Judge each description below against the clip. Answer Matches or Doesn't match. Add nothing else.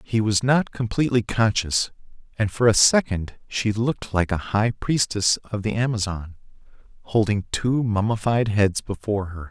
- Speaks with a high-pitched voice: Doesn't match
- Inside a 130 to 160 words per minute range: Matches